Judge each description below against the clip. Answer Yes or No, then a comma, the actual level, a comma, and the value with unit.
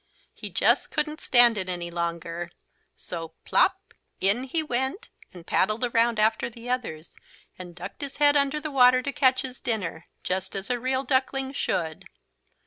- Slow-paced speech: No, average, 165 wpm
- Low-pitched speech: No, high, 240 Hz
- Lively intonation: Yes, wide, 6.5 semitones